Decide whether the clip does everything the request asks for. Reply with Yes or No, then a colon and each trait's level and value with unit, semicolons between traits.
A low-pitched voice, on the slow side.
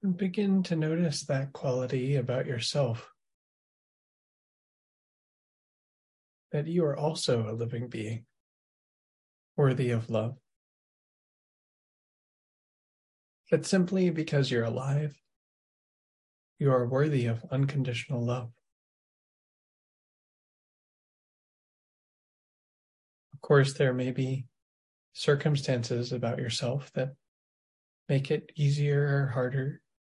Yes: low, 130 Hz; slow, 85 wpm